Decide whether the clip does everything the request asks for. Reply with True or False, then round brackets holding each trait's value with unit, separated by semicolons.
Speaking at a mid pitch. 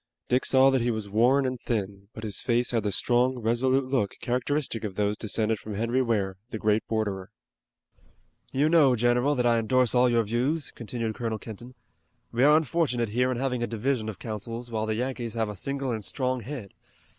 False (120 Hz)